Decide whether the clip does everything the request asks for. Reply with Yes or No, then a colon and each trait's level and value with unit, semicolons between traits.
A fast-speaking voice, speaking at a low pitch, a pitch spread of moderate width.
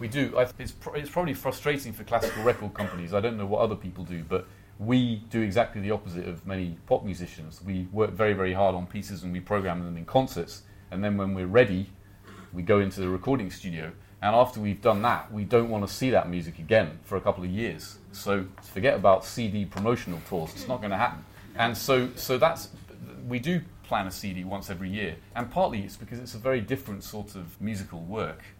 Yes: fast, 215 wpm; low, 100 Hz; average, 3.7 semitones